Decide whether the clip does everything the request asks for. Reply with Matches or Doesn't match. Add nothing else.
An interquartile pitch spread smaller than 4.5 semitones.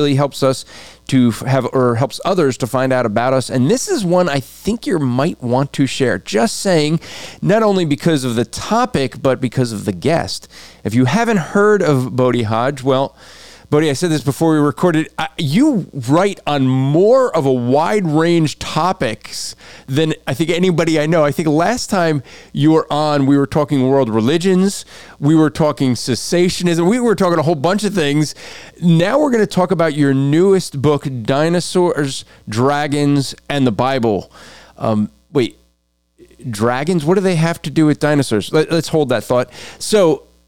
Doesn't match